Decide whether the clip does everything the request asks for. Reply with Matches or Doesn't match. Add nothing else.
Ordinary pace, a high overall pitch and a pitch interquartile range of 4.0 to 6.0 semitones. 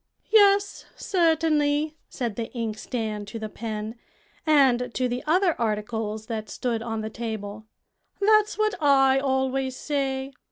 Doesn't match